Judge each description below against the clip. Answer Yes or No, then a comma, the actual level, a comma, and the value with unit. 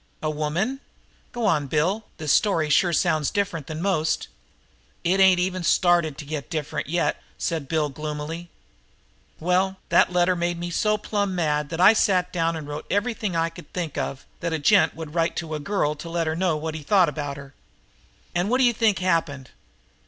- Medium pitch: Yes, medium, 165 Hz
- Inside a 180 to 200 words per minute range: Yes, average, 190 wpm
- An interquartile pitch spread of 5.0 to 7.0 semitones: No, average, 3.3 semitones